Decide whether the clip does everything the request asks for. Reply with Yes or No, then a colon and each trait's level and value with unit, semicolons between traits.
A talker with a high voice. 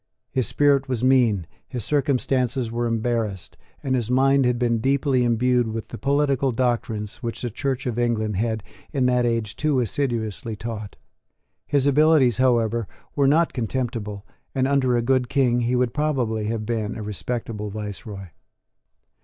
No: low, 120 Hz